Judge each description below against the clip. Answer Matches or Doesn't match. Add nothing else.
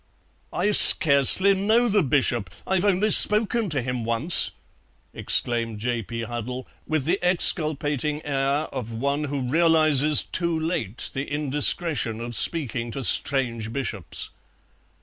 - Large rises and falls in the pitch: Matches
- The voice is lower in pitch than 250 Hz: Matches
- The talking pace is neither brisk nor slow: Doesn't match